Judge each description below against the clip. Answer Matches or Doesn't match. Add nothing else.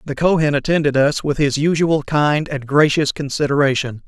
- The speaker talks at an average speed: Matches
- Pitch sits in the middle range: Matches